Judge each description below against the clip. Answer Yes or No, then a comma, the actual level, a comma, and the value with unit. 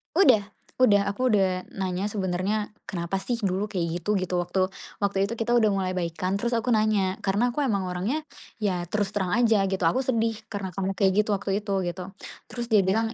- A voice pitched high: Yes, high, 200 Hz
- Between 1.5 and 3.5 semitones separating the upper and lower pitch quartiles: Yes, average, 2.8 semitones